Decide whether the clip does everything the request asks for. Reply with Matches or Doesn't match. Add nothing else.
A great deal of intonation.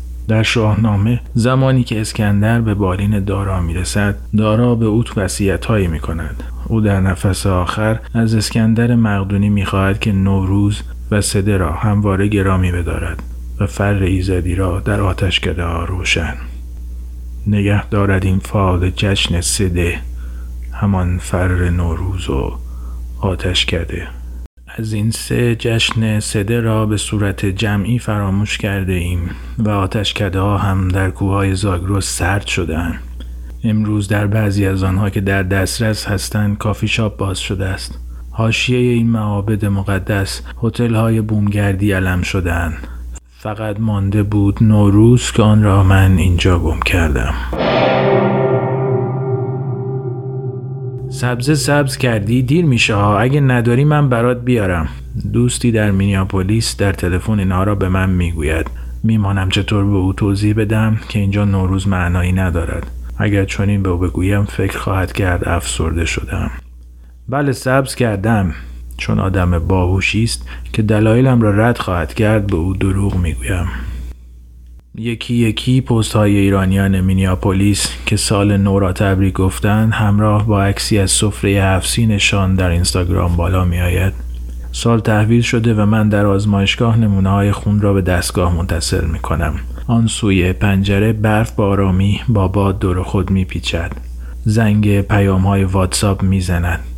Doesn't match